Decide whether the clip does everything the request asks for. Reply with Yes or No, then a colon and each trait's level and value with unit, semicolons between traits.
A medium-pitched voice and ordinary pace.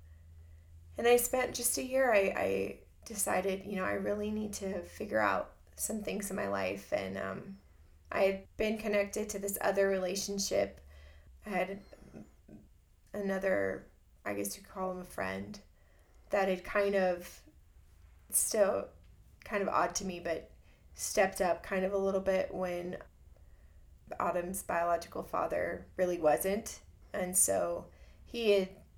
Yes: medium, 175 Hz; average, 145 wpm